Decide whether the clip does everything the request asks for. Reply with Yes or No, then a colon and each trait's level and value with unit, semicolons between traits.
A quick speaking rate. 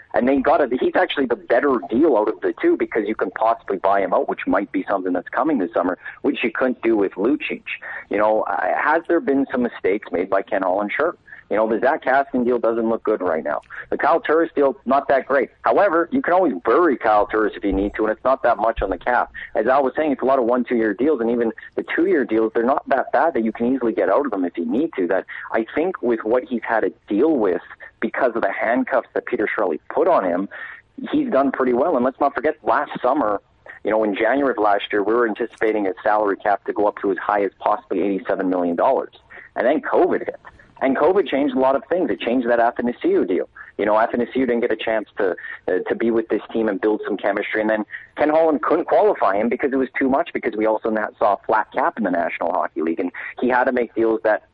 Yes: fast, 260 wpm